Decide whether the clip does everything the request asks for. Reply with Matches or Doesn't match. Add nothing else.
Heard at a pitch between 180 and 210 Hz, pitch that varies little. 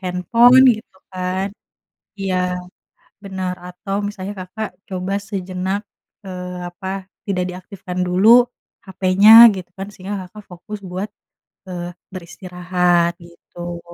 Matches